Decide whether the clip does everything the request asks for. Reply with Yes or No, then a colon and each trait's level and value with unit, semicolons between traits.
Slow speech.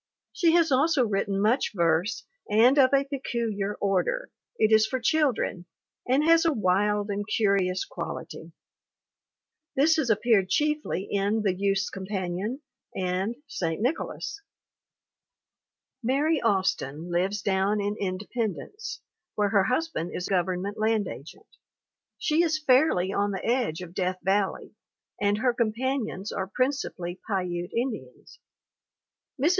Yes: slow, 130 wpm